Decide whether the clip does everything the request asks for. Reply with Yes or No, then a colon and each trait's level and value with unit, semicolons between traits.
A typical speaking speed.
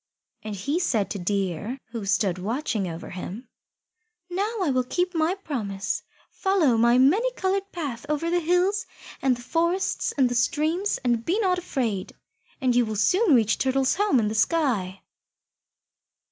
Yes: average, 160 wpm